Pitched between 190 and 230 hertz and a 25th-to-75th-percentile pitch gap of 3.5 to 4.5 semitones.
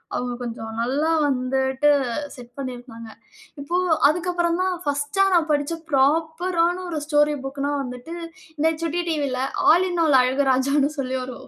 No: very high, 285 Hz; average, 4.0 semitones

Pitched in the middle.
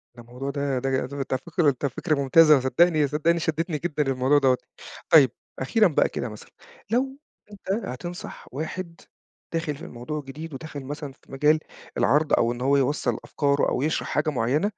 Yes: medium, 145 Hz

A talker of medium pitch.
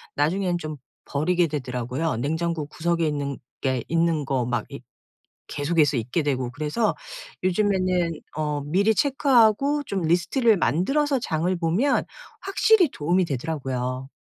Yes: medium, 165 Hz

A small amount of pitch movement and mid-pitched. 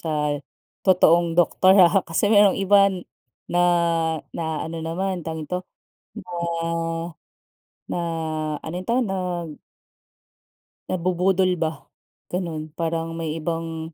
Yes: narrow, 2.3 semitones; medium, 170 Hz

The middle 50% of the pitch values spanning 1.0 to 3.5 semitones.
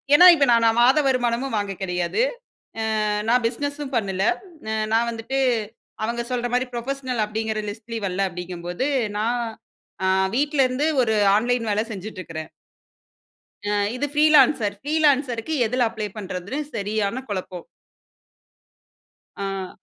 No: average, 4.2 semitones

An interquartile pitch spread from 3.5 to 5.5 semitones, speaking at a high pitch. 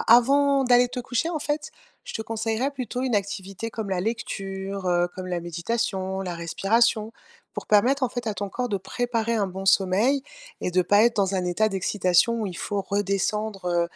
Yes: average, 3.9 semitones; high, 210 Hz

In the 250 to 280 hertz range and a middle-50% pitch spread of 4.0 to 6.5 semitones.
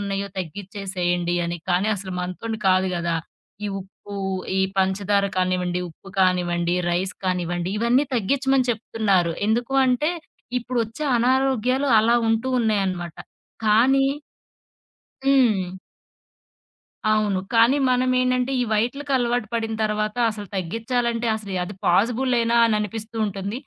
No: high, 215 Hz; average, 4.6 semitones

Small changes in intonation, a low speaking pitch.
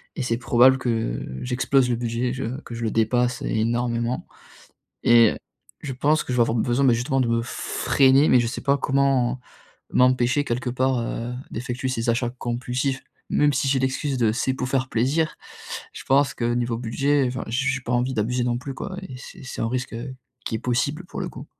Yes: narrow, 2.1 semitones; low, 125 Hz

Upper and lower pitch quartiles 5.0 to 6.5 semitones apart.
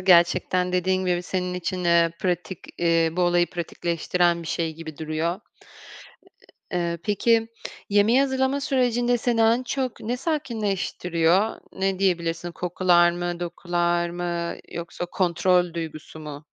No: average, 2.9 semitones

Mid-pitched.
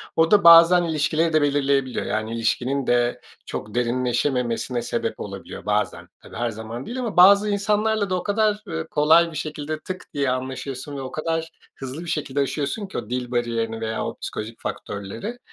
Yes: medium, 145 Hz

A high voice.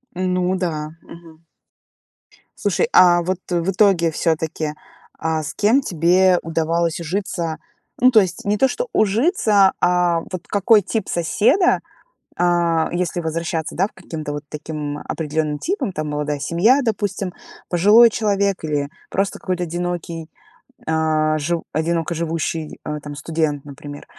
No: medium, 170 Hz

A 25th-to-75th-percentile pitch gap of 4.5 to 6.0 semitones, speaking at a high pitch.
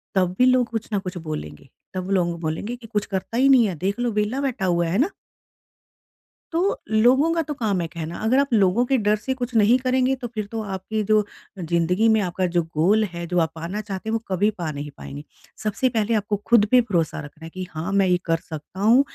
Yes: wide, 5.4 semitones; high, 205 Hz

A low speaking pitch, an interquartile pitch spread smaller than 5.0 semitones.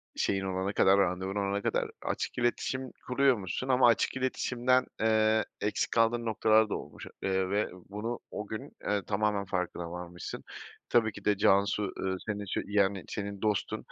Yes: low, 105 Hz; narrow, 2.6 semitones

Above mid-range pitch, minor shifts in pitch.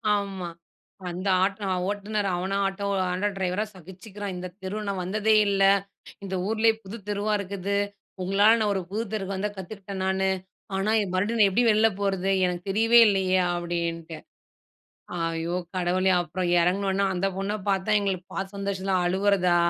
Yes: high, 195 Hz; narrow, 1.8 semitones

